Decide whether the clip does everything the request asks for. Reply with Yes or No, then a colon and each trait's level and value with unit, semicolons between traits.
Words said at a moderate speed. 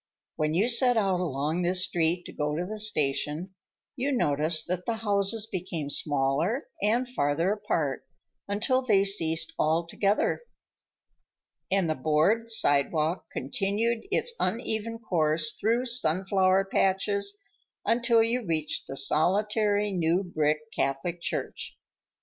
No: slow, 125 wpm